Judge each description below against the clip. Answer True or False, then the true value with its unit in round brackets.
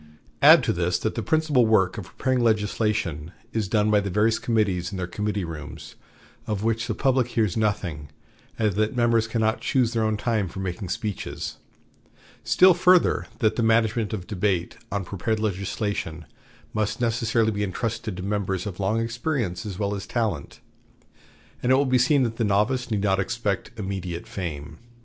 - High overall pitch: False (105 Hz)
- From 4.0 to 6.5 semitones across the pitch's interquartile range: False (3.1 semitones)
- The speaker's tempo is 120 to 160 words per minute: False (175 wpm)